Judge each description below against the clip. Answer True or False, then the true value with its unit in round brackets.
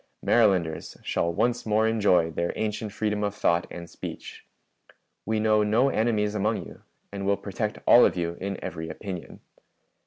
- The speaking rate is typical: True (160 wpm)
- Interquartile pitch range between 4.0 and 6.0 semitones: False (3.4 semitones)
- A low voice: True (105 Hz)